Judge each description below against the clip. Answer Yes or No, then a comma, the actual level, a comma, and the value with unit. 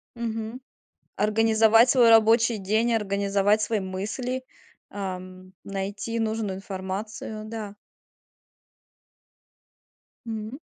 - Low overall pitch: No, high, 215 Hz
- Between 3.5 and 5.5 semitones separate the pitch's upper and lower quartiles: No, narrow, 2.4 semitones